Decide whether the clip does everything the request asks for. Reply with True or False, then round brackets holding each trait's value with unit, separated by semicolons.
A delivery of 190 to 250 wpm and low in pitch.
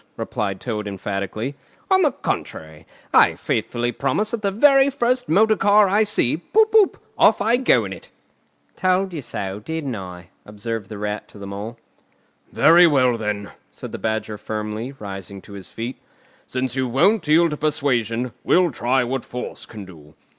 False (170 wpm; 125 Hz)